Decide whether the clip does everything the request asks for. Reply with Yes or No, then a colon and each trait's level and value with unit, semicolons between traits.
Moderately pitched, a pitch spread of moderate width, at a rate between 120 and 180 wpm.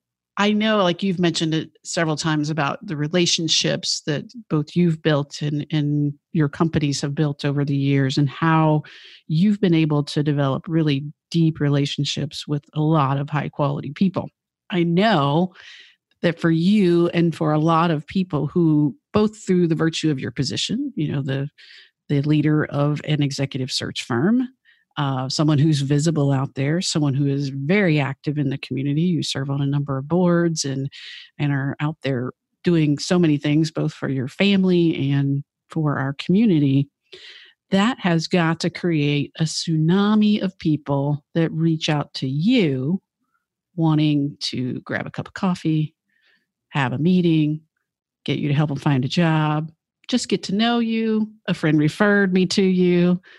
Yes: medium, 155 Hz; average, 3.7 semitones; average, 170 wpm